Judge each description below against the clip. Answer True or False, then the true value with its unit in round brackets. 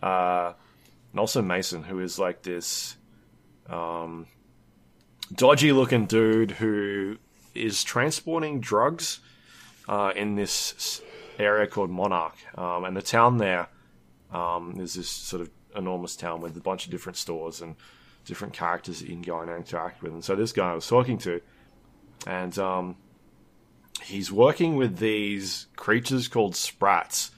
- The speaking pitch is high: False (95 Hz)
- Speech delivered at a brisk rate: False (145 wpm)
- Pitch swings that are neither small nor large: True (4.3 semitones)